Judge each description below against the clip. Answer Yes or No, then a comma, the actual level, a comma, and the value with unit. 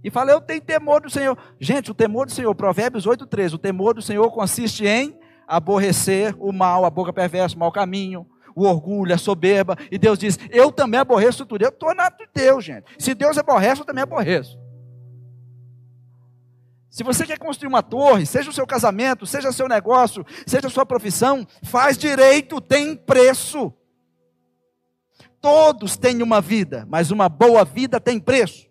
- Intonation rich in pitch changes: Yes, wide, 6.5 semitones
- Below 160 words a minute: No, average, 180 wpm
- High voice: Yes, high, 220 Hz